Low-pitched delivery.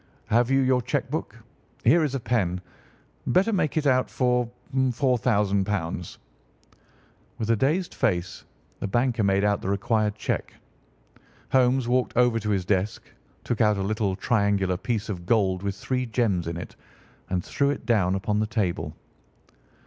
Yes: low, 110 Hz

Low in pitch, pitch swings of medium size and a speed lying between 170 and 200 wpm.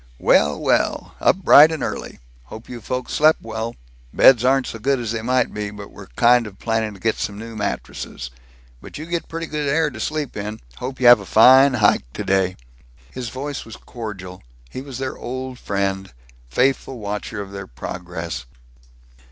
Yes: low, 115 Hz; average, 4.4 semitones; average, 185 wpm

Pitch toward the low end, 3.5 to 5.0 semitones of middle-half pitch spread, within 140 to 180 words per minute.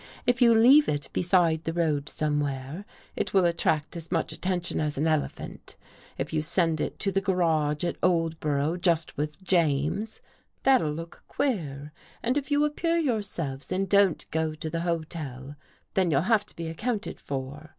No: medium, 165 Hz; average, 4.4 semitones; average, 170 wpm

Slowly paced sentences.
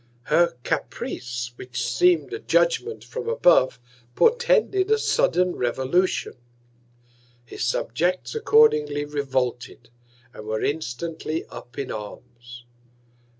Yes: slow, 100 wpm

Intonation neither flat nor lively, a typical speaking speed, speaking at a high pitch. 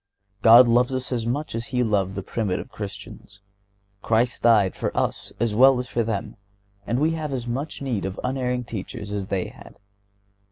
No: average, 3.5 semitones; average, 185 wpm; low, 115 Hz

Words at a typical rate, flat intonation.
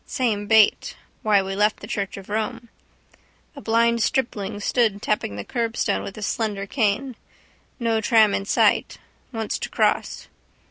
Yes: average, 150 wpm; narrow, 2.3 semitones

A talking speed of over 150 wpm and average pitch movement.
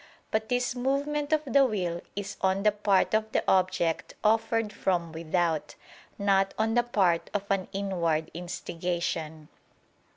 No: average, 140 wpm; average, 4.3 semitones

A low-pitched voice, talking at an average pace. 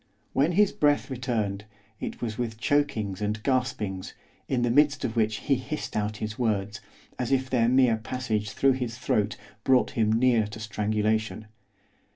Yes: low, 115 Hz; average, 165 wpm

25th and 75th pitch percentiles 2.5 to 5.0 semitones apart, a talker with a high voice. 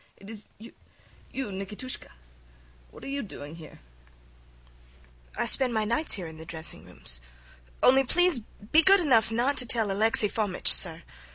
No: wide, 5.5 semitones; high, 220 Hz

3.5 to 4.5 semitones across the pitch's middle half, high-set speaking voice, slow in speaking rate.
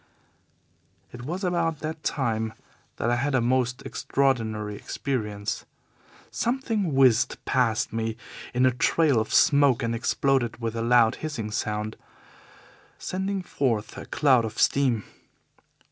No: average, 4.0 semitones; low, 125 Hz; slow, 130 wpm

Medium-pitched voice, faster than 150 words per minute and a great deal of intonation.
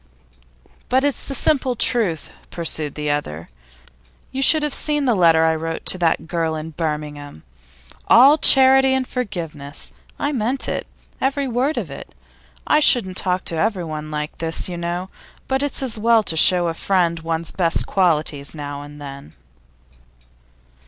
Yes: medium, 175 Hz; average, 160 wpm; wide, 8.4 semitones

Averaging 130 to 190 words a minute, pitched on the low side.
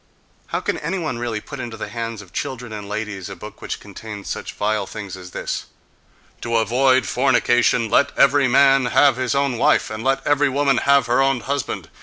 No: average, 200 wpm; low, 120 Hz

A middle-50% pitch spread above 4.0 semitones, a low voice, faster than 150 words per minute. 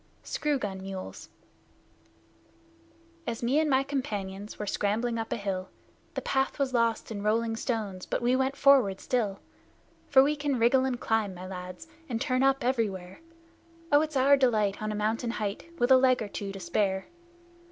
No: average, 4.8 semitones; high, 230 Hz; average, 175 wpm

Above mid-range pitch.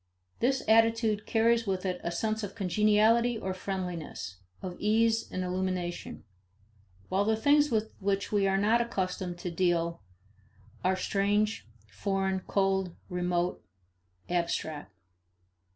Yes: high, 195 Hz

